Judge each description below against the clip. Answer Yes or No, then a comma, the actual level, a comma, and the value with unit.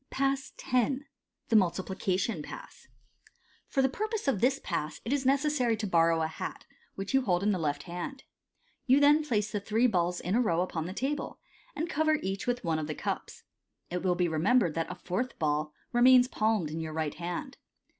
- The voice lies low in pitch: No, high, 205 Hz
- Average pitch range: No, wide, 7.4 semitones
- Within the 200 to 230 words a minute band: Yes, fast, 205 wpm